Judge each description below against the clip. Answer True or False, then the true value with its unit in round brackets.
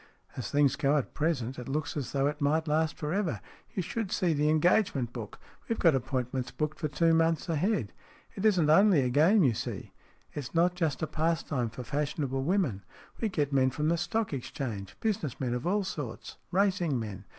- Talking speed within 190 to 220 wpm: True (205 wpm)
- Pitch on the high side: False (150 Hz)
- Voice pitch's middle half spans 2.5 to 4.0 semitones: False (4.6 semitones)